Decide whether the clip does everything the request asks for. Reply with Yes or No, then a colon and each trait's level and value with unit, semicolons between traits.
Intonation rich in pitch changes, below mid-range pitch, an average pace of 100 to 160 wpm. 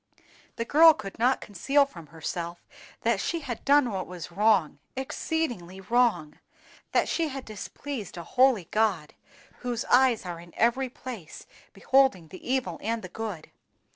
No: wide, 6.6 semitones; high, 225 Hz; average, 145 wpm